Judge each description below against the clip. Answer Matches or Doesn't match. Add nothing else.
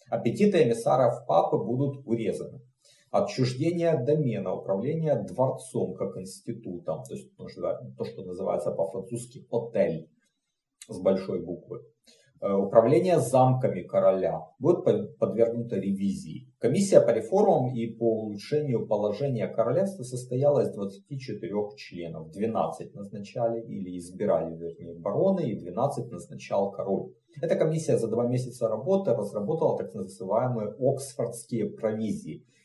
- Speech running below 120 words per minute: Matches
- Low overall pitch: Matches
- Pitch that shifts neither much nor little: Doesn't match